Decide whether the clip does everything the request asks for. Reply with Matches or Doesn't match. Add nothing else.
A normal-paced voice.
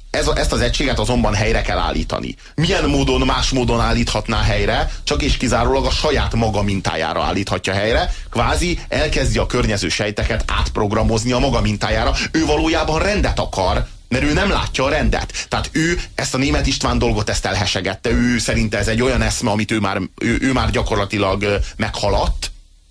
Doesn't match